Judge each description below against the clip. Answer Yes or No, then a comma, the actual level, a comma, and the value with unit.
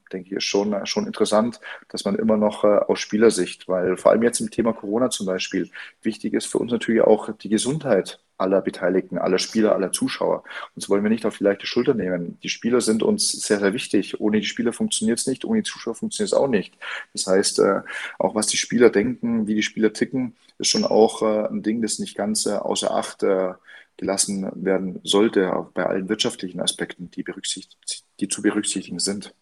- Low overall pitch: Yes, low, 110 Hz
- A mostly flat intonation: No, average, 3.2 semitones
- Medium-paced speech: No, fast, 205 wpm